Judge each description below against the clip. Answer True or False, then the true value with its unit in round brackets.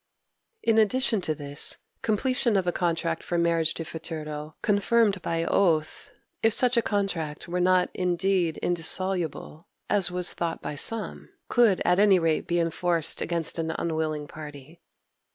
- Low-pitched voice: False (175 Hz)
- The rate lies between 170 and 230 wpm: False (150 wpm)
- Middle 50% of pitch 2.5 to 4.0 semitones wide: True (3.5 semitones)